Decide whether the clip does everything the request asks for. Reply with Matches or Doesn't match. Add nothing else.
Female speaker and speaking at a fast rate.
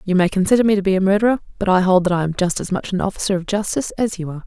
Matches